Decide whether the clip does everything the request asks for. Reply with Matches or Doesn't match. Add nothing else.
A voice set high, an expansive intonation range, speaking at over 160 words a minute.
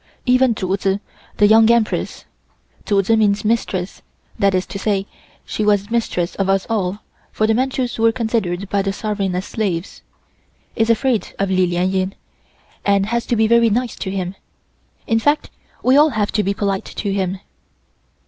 Doesn't match